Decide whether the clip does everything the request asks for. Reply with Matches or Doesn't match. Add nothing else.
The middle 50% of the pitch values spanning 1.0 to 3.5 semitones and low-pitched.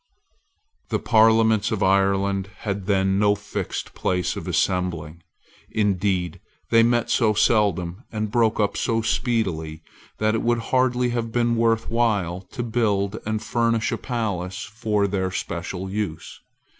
Matches